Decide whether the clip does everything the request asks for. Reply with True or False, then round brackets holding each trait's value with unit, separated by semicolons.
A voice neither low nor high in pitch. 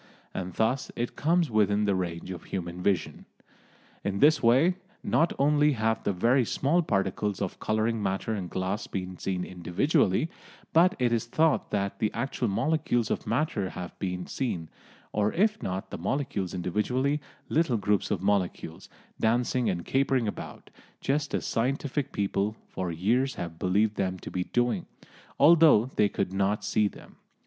False (105 Hz)